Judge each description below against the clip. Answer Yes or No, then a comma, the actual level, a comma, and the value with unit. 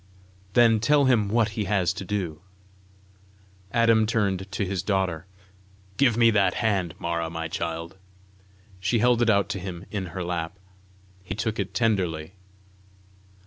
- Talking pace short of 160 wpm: Yes, average, 145 wpm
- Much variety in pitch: No, average, 3.9 semitones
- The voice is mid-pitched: No, low, 100 Hz